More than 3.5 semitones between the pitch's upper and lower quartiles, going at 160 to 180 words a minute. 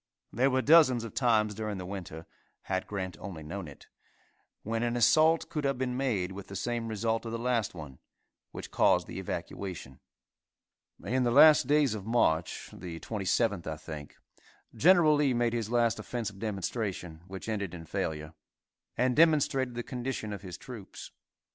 Yes: average, 5.0 semitones; average, 165 wpm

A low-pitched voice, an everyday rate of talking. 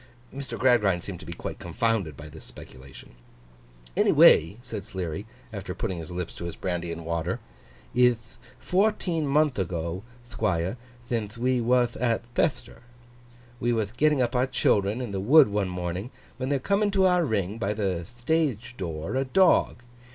Yes: low, 110 Hz; average, 165 wpm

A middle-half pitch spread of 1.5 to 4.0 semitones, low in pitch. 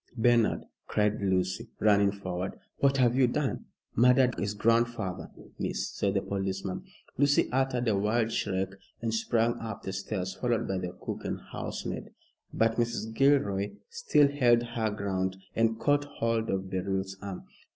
Yes: average, 3.7 semitones; low, 110 Hz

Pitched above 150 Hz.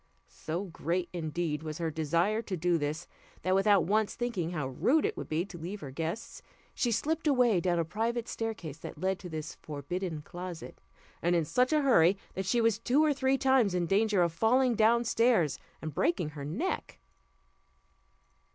Yes: medium, 185 Hz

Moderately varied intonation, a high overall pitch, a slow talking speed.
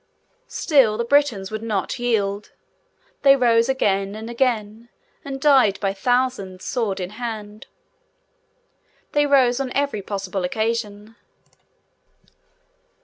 Yes: average, 4.0 semitones; high, 225 Hz; slow, 110 wpm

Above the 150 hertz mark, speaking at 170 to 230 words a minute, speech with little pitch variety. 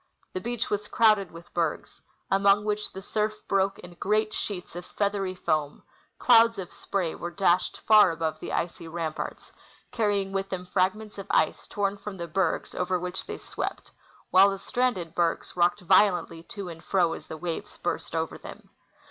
No: high, 190 Hz; average, 175 wpm; average, 3.0 semitones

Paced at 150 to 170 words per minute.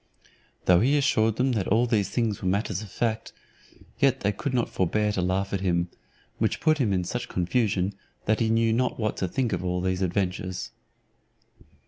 No: average, 190 wpm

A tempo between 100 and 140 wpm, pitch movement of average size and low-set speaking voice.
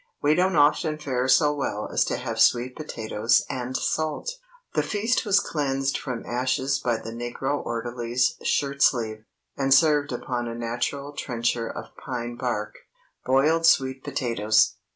No: average, 150 wpm; average, 3.5 semitones; low, 130 Hz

